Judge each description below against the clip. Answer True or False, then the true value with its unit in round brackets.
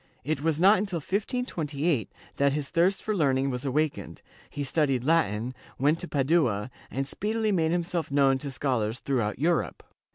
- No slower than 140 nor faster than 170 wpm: True (165 wpm)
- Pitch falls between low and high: True (145 Hz)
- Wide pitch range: False (4.4 semitones)